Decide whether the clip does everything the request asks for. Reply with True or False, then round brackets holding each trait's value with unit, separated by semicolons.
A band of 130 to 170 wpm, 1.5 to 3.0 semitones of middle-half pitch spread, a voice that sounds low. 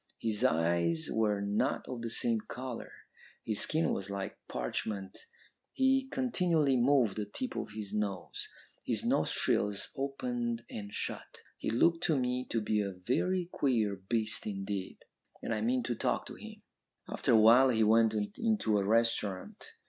False (155 wpm; 4.1 semitones; 115 Hz)